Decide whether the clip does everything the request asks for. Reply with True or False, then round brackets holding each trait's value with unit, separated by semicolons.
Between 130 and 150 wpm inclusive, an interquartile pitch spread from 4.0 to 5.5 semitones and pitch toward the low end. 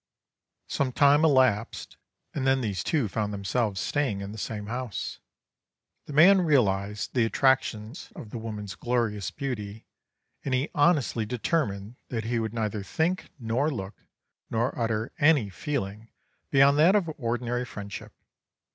True (140 wpm; 4.8 semitones; 120 Hz)